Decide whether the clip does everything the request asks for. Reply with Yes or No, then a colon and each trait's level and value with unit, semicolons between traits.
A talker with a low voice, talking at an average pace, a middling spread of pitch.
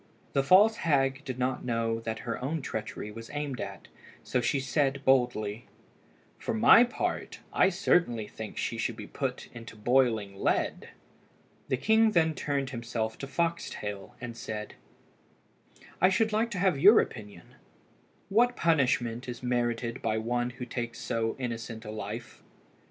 Yes: low, 125 Hz; average, 150 wpm; average, 4.4 semitones